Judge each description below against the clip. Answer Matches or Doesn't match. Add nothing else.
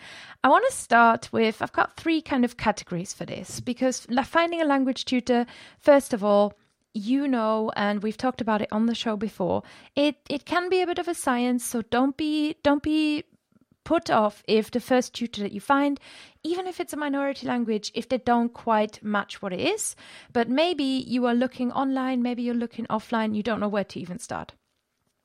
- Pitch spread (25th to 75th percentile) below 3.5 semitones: Doesn't match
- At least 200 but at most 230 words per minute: Matches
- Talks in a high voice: Matches